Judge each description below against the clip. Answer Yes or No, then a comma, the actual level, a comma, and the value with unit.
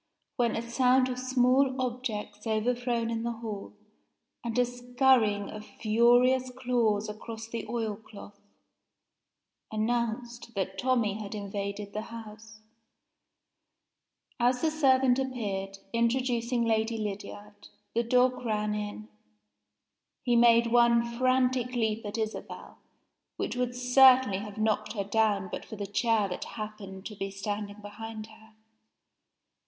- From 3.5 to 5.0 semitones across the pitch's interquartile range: No, average, 2.8 semitones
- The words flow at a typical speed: No, slow, 125 wpm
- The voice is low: No, high, 230 Hz